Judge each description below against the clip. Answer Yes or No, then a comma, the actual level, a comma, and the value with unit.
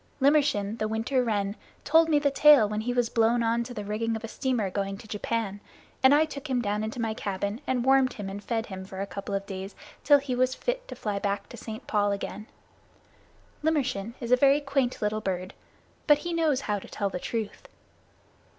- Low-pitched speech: No, high, 225 Hz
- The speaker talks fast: Yes, fast, 215 wpm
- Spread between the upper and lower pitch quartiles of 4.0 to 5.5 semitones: Yes, average, 4.6 semitones